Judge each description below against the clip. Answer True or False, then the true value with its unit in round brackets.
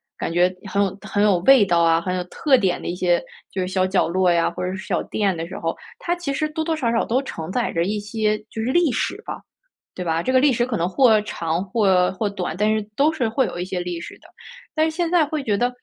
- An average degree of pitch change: False (6.1 semitones)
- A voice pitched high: True (205 Hz)